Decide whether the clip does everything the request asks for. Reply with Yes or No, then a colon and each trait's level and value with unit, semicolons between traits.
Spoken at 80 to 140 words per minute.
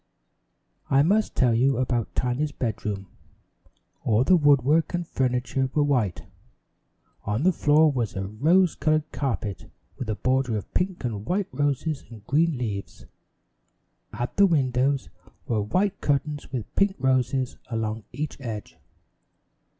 Yes: slow, 135 wpm